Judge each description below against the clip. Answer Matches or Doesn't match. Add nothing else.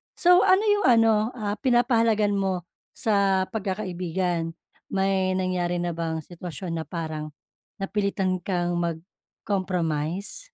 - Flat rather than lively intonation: Doesn't match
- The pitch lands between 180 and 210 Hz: Matches